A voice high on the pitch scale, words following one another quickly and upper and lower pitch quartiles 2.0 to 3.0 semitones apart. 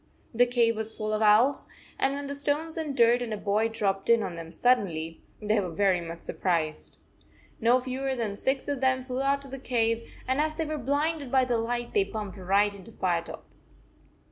No: high, 235 Hz; fast, 210 wpm; average, 4.8 semitones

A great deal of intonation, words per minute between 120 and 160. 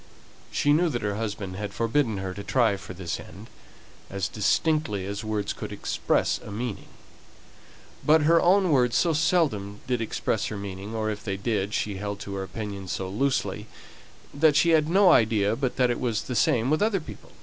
No: wide, 6.5 semitones; average, 190 wpm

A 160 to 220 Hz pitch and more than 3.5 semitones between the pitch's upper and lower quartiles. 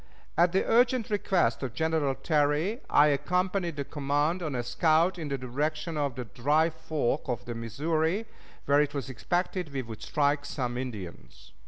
No: medium, 150 Hz; average, 4.2 semitones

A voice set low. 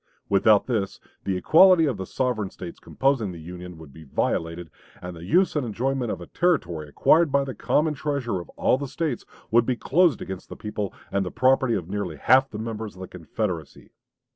Yes: low, 110 Hz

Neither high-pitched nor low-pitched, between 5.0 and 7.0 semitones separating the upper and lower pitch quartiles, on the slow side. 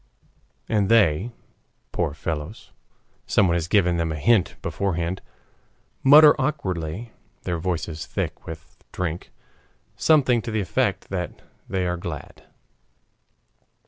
No: very low, 90 Hz; average, 5.3 semitones; slow, 115 wpm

